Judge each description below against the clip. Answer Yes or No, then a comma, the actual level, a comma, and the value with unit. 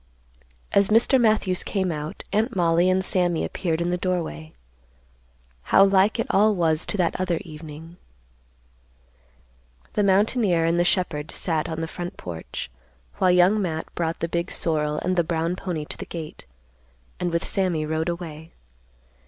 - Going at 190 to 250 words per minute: No, average, 160 wpm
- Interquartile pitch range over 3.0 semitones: No, average, 2.7 semitones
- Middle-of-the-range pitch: Yes, medium, 175 Hz